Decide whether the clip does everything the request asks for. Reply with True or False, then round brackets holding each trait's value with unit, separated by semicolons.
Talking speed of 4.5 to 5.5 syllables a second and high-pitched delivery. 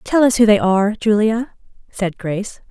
True (5.0 syllables/s; 210 Hz)